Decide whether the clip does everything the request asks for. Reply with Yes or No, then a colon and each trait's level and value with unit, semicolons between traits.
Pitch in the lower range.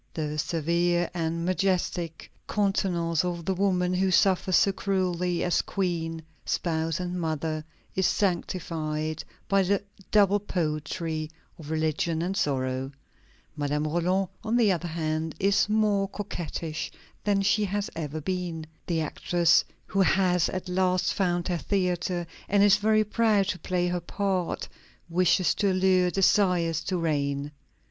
No: medium, 175 Hz